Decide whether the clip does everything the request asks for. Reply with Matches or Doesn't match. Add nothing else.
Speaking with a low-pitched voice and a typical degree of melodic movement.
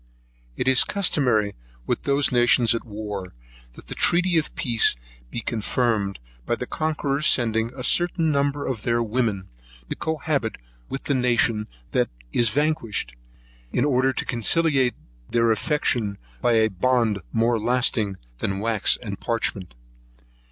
Matches